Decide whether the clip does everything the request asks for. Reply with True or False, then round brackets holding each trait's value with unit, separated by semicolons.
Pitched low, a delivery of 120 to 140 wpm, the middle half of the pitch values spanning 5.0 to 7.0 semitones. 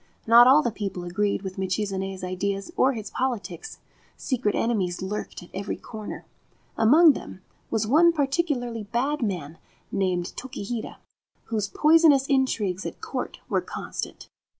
False (215 Hz; 135 wpm; 5.4 semitones)